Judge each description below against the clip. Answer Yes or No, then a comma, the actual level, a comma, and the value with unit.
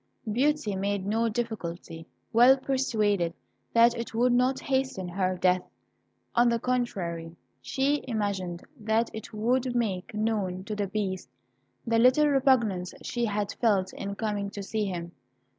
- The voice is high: Yes, high, 215 Hz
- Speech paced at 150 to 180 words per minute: No, average, 140 wpm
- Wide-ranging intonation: No, average, 4.1 semitones